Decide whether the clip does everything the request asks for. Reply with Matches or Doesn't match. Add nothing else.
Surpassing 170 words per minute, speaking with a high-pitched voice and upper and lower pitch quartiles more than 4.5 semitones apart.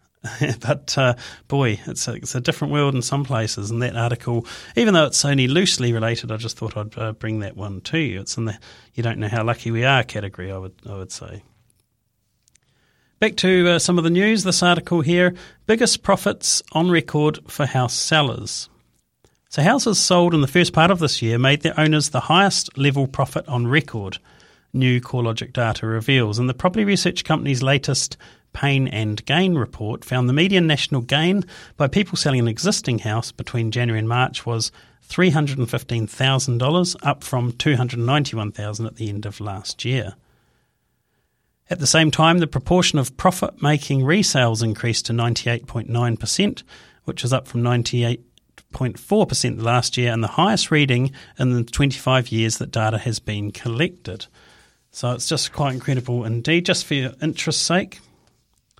Doesn't match